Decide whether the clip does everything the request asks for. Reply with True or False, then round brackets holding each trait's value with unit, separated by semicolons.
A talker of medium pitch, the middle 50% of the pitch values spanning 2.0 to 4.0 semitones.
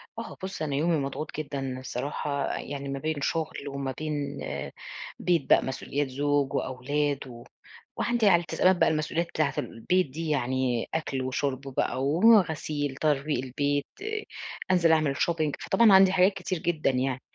True (145 Hz; 3.4 semitones)